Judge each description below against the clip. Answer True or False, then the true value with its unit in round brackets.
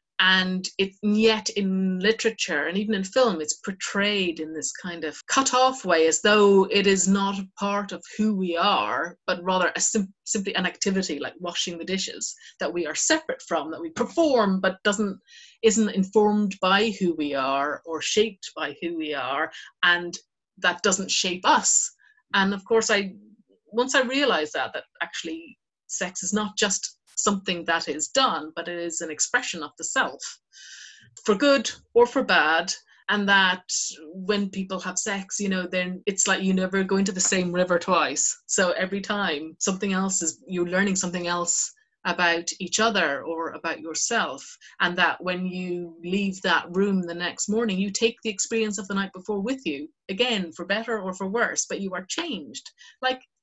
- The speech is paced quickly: False (185 wpm)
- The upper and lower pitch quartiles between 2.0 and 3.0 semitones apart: False (3.4 semitones)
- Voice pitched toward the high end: True (195 Hz)